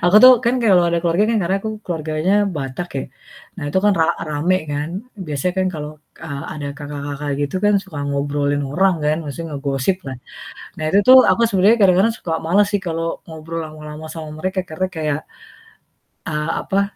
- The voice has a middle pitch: Yes, medium, 160 Hz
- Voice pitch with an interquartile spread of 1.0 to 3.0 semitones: No, average, 4.3 semitones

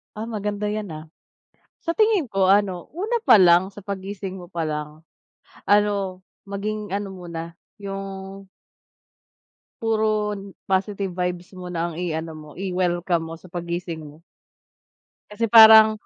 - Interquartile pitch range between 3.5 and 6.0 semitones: No, average, 3.0 semitones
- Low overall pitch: No, high, 195 Hz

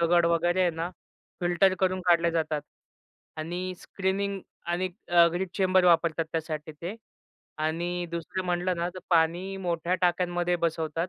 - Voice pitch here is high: No, medium, 175 Hz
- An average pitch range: No, narrow, 1.8 semitones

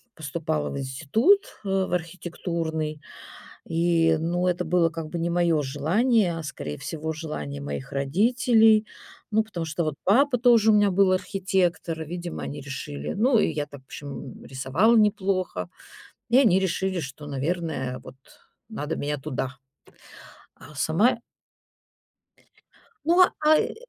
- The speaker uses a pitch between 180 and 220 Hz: No, medium, 170 Hz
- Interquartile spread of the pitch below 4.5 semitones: No, average, 5.1 semitones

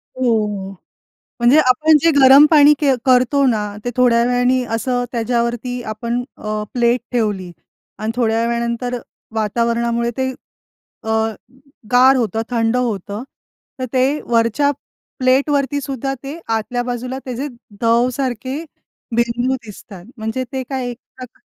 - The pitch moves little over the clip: Yes, narrow, 2.1 semitones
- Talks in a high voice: Yes, high, 245 Hz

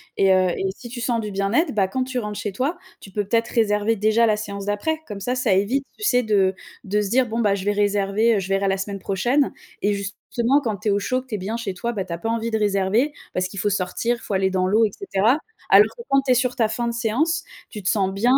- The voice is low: No, high, 210 Hz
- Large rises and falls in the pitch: No, average, 3.3 semitones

